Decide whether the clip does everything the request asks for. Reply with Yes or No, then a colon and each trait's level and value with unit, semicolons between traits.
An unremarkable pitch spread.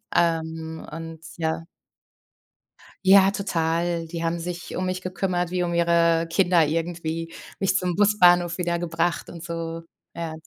No: narrow, 1.3 semitones